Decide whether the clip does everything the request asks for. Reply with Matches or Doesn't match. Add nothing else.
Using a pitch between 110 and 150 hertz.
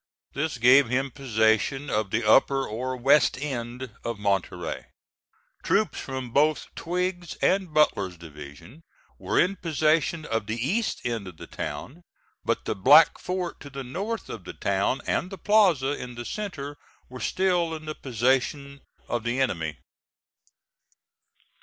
Matches